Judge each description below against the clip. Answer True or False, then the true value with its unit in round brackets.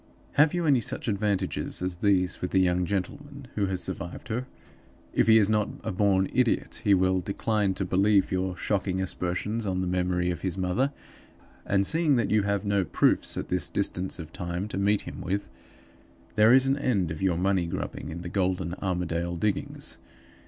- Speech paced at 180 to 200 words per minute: True (190 wpm)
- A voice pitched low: True (95 Hz)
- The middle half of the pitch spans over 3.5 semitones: False (2.7 semitones)